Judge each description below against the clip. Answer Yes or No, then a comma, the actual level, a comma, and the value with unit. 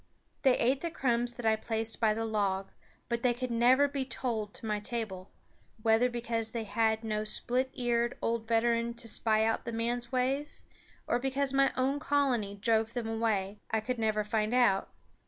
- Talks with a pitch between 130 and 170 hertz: No, high, 230 Hz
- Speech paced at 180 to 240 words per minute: Yes, average, 185 wpm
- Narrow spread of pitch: Yes, narrow, 2.2 semitones